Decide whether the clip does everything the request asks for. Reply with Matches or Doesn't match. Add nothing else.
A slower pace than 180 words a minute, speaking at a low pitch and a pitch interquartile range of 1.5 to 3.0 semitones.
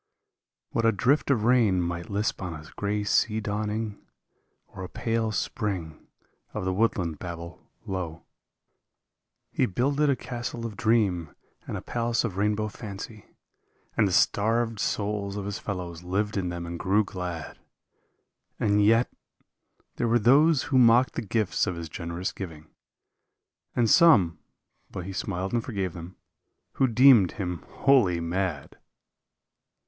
Doesn't match